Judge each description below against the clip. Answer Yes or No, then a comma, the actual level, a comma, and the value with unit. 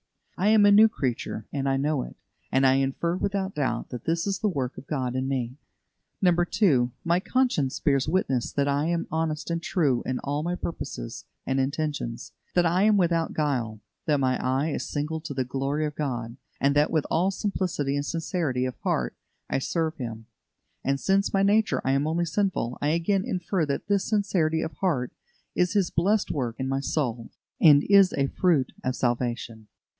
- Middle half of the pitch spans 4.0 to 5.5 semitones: Yes, average, 5.1 semitones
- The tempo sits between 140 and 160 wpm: No, average, 190 wpm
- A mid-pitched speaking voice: Yes, medium, 150 Hz